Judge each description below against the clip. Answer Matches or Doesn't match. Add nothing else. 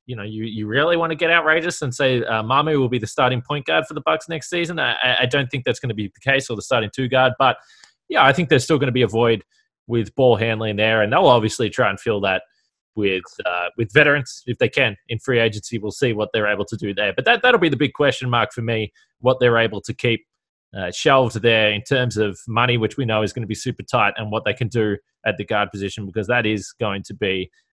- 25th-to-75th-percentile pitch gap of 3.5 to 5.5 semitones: Matches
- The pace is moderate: Doesn't match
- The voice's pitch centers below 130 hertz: Matches